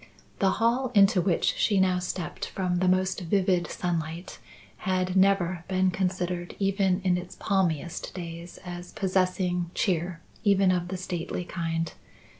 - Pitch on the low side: No, medium, 185 Hz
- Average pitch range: No, narrow, 1.5 semitones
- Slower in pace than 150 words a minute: Yes, average, 140 wpm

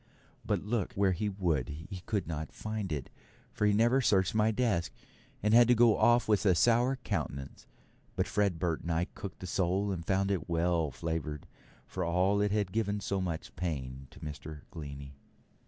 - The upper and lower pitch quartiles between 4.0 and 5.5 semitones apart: Yes, average, 4.3 semitones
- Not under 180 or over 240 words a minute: Yes, average, 190 wpm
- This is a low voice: Yes, very low, 95 Hz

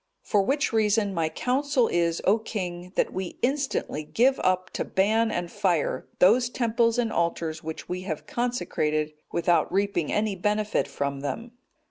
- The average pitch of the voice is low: No, high, 195 Hz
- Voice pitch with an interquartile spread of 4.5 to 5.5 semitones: Yes, average, 5.1 semitones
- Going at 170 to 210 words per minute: No, average, 155 wpm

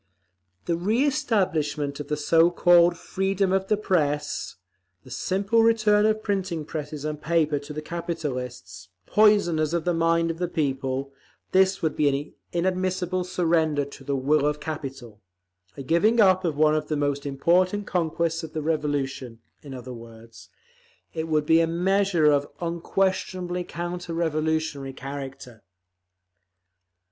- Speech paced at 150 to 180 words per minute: No, average, 140 wpm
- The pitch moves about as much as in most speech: Yes, average, 4.0 semitones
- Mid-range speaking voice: Yes, medium, 160 Hz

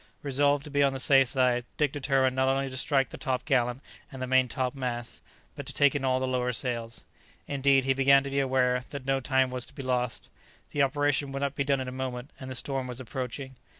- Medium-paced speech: No, fast, 245 wpm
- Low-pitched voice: Yes, low, 130 Hz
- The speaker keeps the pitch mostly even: Yes, narrow, 1.4 semitones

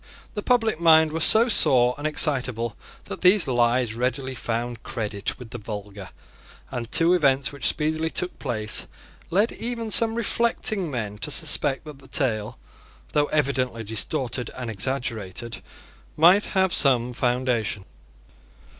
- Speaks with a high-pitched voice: No, low, 130 Hz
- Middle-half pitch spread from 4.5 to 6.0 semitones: Yes, wide, 5.4 semitones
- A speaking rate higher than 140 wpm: No, slow, 135 wpm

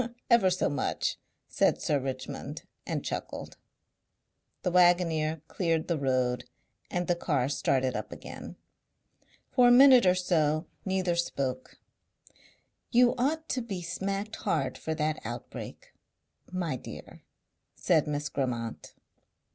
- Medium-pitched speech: Yes, medium, 170 Hz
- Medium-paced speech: No, slow, 125 wpm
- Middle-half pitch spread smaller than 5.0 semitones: No, average, 5.3 semitones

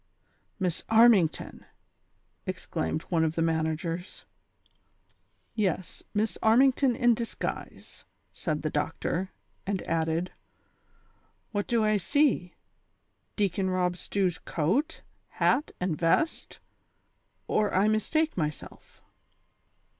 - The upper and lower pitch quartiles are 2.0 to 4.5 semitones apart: No, average, 5.2 semitones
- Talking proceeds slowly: Yes, slow, 105 wpm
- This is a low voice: No, medium, 185 Hz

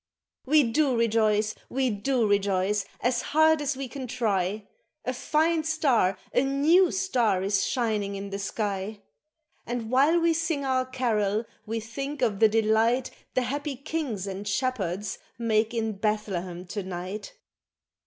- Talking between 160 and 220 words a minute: No, average, 145 wpm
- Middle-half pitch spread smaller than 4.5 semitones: No, average, 4.9 semitones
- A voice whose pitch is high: Yes, high, 225 Hz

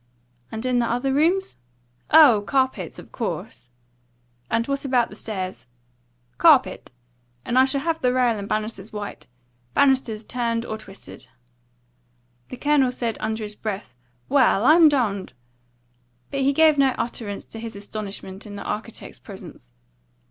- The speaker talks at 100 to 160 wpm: Yes, average, 145 wpm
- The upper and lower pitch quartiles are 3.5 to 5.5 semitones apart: Yes, average, 4.3 semitones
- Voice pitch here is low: No, high, 235 Hz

